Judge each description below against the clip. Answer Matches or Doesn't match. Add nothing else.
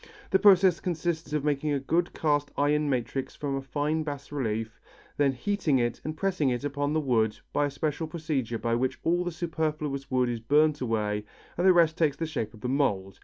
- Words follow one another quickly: Matches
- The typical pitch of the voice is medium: Matches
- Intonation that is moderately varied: Matches